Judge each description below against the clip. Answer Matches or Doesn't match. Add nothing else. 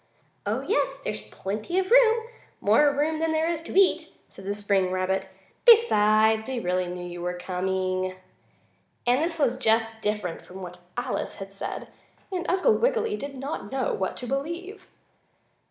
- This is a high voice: Matches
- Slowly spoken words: Doesn't match